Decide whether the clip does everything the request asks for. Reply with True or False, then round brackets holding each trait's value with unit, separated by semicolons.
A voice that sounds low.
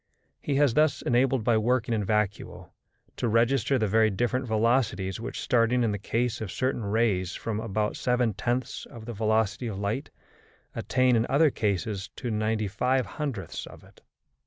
True (115 Hz)